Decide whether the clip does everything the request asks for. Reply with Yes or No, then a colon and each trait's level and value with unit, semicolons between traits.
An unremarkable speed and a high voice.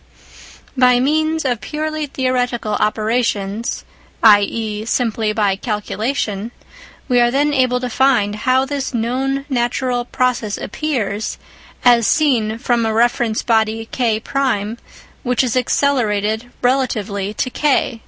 No: slow, 115 wpm; high, 240 Hz